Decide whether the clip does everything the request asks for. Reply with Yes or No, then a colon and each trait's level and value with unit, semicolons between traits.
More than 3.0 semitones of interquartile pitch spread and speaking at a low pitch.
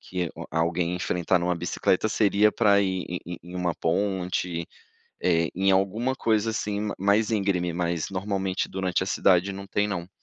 No: narrow, 2.5 semitones; very low, 95 Hz